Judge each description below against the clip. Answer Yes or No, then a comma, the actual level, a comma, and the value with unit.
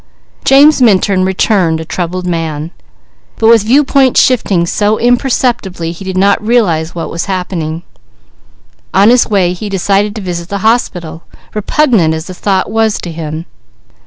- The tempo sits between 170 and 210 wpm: No, average, 150 wpm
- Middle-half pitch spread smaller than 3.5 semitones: No, average, 4.6 semitones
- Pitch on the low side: No, high, 190 Hz